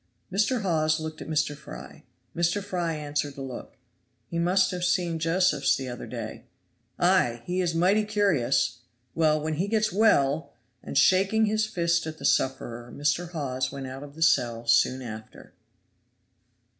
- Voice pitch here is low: No, medium, 160 Hz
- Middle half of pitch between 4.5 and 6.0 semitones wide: Yes, average, 5.3 semitones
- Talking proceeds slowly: No, average, 160 wpm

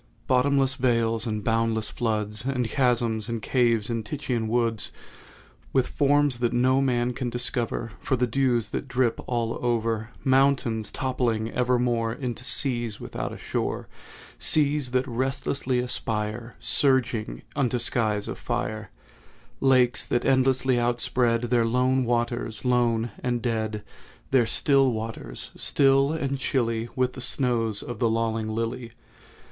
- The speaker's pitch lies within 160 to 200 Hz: No, low, 120 Hz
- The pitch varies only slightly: Yes, narrow, 2.2 semitones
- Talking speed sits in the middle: No, slow, 130 wpm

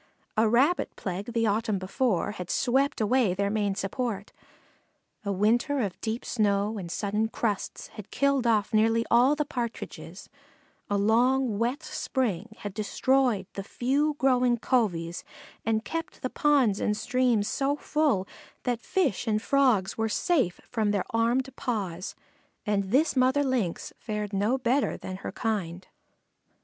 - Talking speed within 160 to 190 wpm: No, average, 150 wpm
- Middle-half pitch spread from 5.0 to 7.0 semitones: No, average, 4.1 semitones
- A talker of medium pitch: No, high, 225 Hz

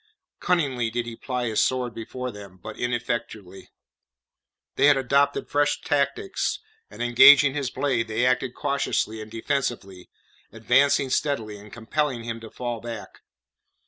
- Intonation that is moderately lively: Yes, average, 3.6 semitones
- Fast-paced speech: No, average, 140 wpm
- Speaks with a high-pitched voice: No, low, 120 Hz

